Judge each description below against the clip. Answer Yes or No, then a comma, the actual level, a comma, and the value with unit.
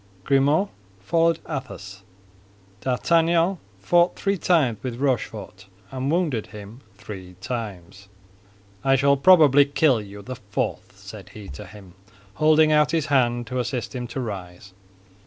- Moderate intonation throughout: No, wide, 6.7 semitones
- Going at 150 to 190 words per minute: No, slow, 135 wpm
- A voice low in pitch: Yes, low, 130 Hz